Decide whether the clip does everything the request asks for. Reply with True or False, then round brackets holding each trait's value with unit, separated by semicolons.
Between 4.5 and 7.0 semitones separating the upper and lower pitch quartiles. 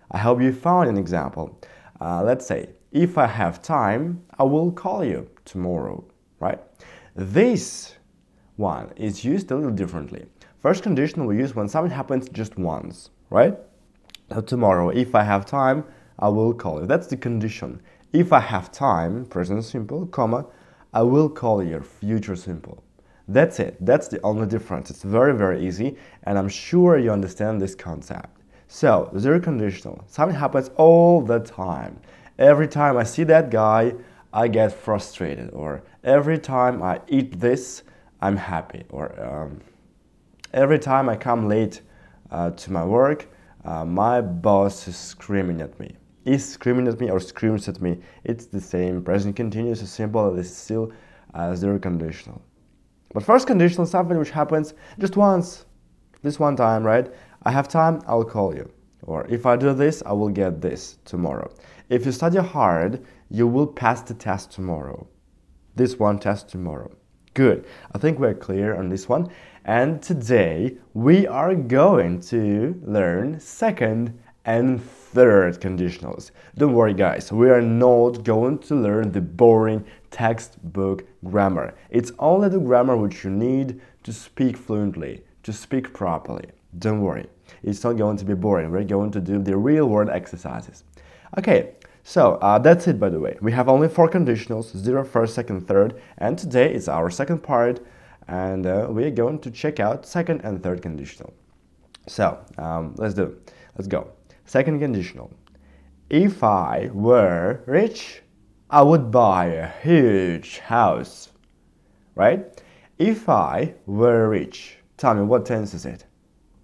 True (5.4 semitones)